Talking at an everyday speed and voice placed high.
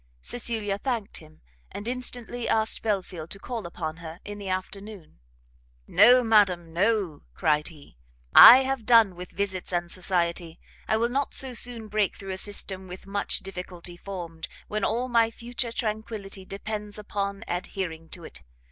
Yes: average, 155 wpm; high, 200 Hz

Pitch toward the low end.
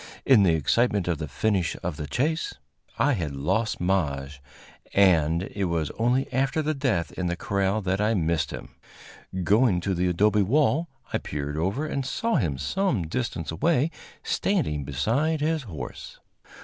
Yes: low, 100 Hz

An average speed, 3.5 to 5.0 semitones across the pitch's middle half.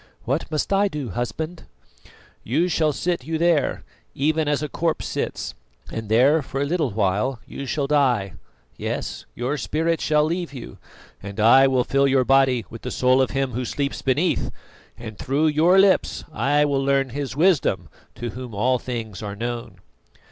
Yes: average, 175 wpm; average, 4.1 semitones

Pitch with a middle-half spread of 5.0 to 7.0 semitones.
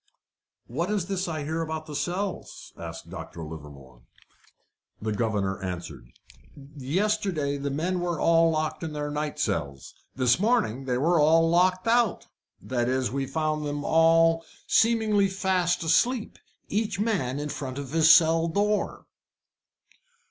Yes: wide, 5.4 semitones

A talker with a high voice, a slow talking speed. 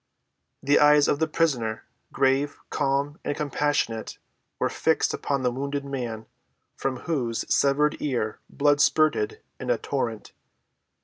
No: medium, 140 Hz; slow, 130 wpm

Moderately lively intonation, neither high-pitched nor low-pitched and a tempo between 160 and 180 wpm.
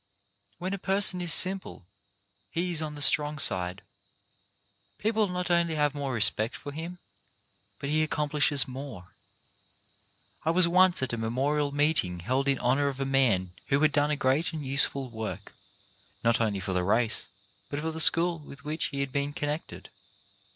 Yes: average, 4.0 semitones; medium, 145 Hz; average, 170 wpm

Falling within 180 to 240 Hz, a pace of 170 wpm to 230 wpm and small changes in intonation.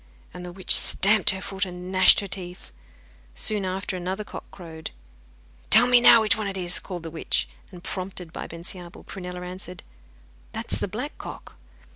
Yes: medium, 185 Hz; average, 180 wpm; narrow, 2.0 semitones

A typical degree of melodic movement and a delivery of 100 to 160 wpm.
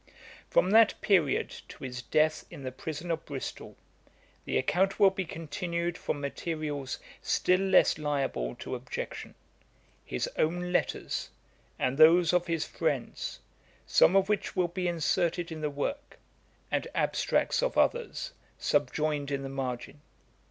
Yes: average, 3.8 semitones; average, 140 wpm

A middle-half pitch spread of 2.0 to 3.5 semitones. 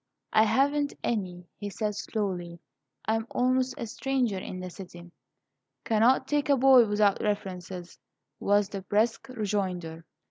No: average, 4.9 semitones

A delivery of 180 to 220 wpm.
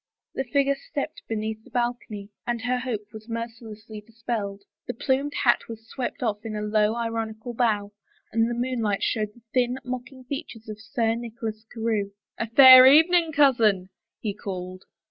No: average, 165 wpm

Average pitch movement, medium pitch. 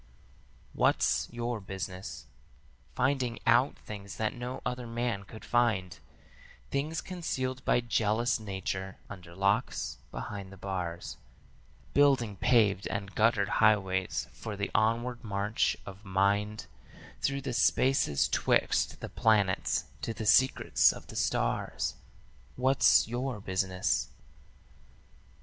No: average, 3.9 semitones; low, 110 Hz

